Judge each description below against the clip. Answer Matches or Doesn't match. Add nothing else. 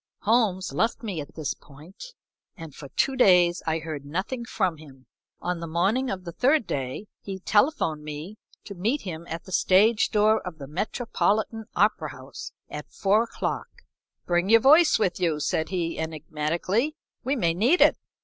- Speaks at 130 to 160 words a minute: Doesn't match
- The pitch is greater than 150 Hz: Matches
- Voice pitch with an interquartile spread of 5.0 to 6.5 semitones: Matches